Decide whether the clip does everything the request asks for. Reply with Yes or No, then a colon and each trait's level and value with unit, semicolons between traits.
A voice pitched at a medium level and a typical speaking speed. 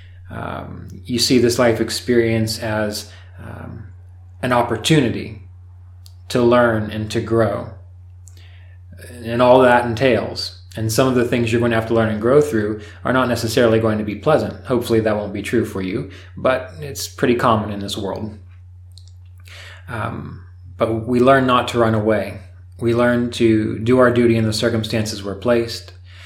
No: low, 110 Hz; average, 165 wpm